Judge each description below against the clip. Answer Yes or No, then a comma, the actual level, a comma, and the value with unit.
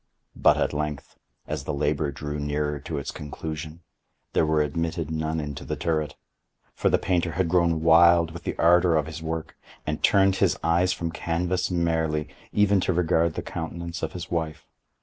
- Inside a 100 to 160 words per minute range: No, average, 180 wpm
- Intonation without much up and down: Yes, narrow, 1.9 semitones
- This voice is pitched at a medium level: No, very low, 80 Hz